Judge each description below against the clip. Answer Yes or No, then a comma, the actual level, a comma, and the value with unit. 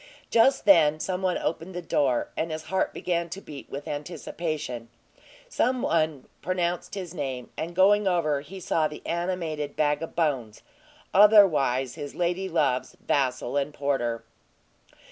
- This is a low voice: No, medium, 160 Hz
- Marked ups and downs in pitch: No, average, 4.1 semitones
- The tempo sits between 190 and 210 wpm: No, average, 145 wpm